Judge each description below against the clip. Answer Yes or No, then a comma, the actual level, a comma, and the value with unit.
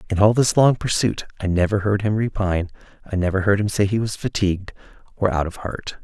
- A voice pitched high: No, low, 100 Hz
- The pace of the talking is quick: Yes, fast, 220 wpm